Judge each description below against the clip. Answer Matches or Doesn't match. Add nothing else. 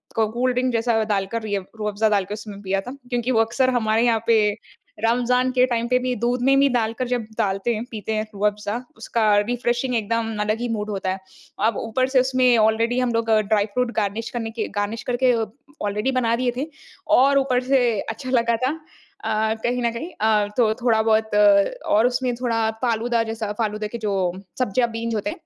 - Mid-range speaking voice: Doesn't match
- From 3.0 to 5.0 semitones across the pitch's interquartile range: Doesn't match